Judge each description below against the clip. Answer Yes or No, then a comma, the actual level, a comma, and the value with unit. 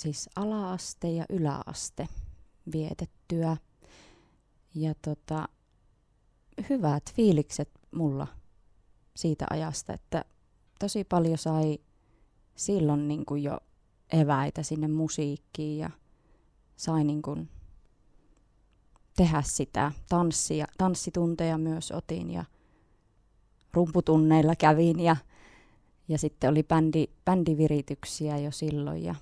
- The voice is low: No, medium, 155 Hz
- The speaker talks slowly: Yes, slow, 90 wpm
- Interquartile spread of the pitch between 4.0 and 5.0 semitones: No, average, 2.8 semitones